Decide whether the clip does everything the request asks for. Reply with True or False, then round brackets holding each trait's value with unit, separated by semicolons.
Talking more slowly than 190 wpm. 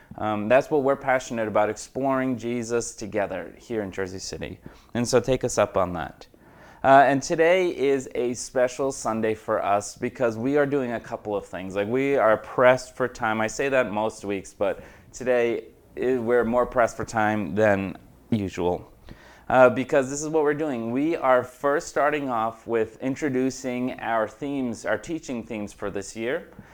True (180 wpm)